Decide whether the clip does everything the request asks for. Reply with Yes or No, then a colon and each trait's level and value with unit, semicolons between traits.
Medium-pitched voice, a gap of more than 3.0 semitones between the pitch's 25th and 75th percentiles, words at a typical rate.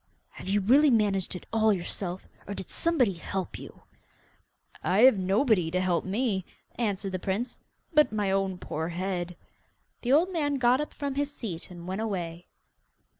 No: high, 200 Hz; average, 5.3 semitones; average, 170 wpm